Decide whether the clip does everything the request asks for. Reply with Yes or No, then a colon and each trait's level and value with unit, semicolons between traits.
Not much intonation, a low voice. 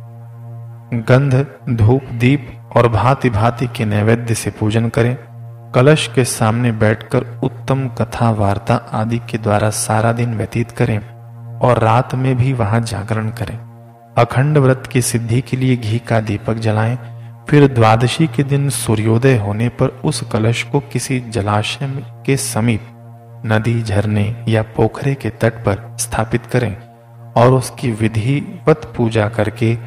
Yes: narrow, 2.0 semitones; low, 115 Hz